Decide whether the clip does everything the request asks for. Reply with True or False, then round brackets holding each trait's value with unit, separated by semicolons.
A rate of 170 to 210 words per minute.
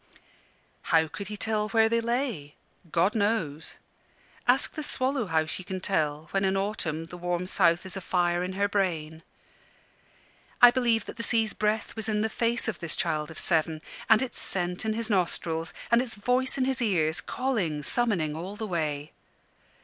True (180 wpm)